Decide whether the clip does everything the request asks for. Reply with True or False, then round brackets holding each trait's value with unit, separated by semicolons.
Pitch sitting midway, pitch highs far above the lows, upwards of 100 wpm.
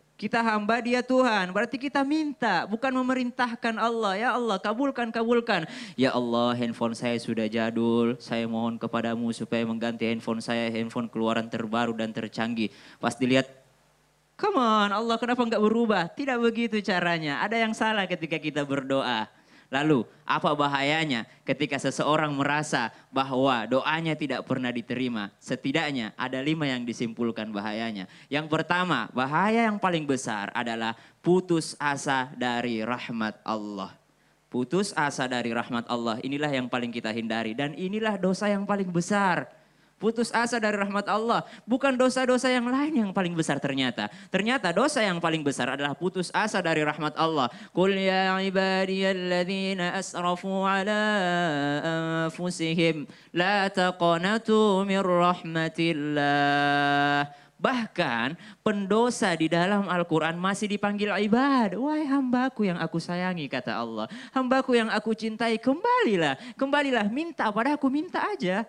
True (170 Hz; 8.8 semitones; 130 wpm)